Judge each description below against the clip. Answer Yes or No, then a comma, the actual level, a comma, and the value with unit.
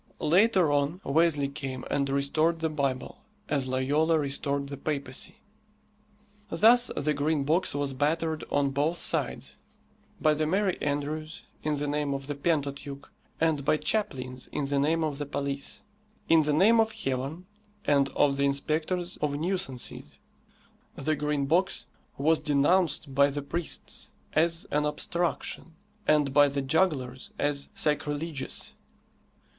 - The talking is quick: No, average, 140 wpm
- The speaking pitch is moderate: Yes, medium, 145 Hz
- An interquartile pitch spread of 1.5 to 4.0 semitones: Yes, narrow, 2.5 semitones